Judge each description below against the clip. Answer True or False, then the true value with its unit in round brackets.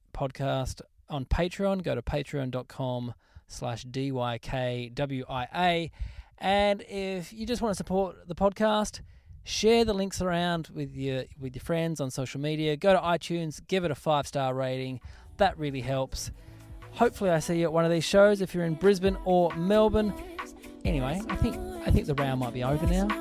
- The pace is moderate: True (175 wpm)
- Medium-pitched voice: True (160 Hz)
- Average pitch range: False (6.7 semitones)